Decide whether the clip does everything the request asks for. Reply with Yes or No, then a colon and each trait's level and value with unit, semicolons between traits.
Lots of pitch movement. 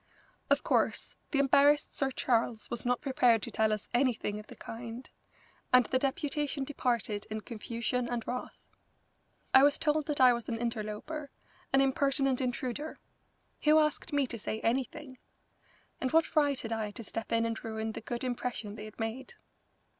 No: average, 3.4 semitones